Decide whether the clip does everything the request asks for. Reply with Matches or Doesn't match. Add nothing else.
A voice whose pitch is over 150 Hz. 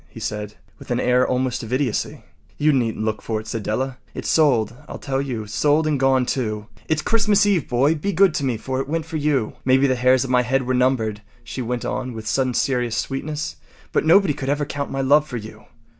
Doesn't match